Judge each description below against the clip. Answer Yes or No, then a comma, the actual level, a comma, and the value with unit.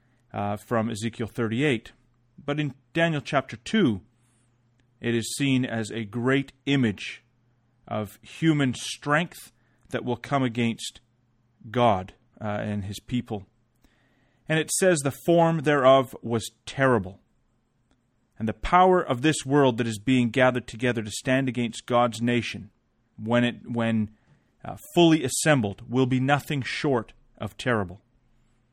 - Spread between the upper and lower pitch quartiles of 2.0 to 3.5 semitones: Yes, narrow, 2.6 semitones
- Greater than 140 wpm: No, slow, 135 wpm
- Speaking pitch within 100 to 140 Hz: Yes, low, 120 Hz